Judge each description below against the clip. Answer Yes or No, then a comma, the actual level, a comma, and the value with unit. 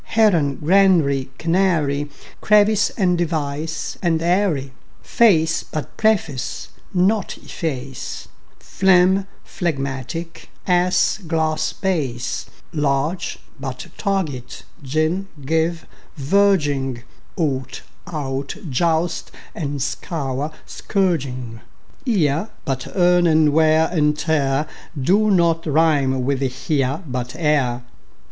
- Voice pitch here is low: No, medium, 155 Hz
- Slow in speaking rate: Yes, slow, 95 wpm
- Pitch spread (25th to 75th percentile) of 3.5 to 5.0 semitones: Yes, average, 4.5 semitones